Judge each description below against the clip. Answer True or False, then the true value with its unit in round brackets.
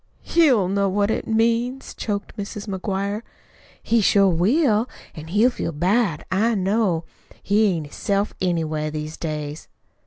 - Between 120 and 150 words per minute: True (145 wpm)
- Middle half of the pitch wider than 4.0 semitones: True (4.7 semitones)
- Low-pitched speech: False (200 Hz)